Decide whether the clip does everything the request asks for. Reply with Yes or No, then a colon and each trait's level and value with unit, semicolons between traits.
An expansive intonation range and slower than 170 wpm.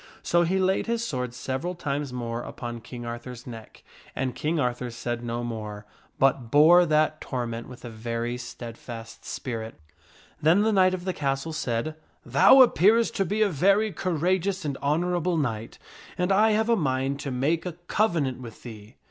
No: wide, 6.9 semitones; average, 180 wpm